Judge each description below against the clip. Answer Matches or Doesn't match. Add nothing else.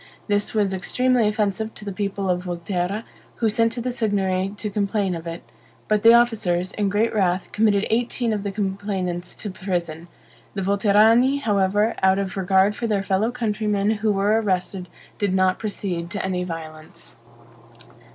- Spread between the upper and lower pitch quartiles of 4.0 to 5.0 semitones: Doesn't match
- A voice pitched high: Matches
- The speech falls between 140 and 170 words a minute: Matches